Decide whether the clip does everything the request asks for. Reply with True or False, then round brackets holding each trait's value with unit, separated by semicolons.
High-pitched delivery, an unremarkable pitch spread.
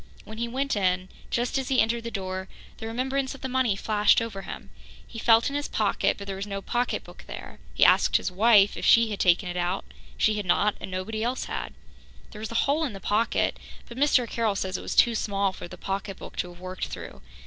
True (215 Hz; 3.5 semitones)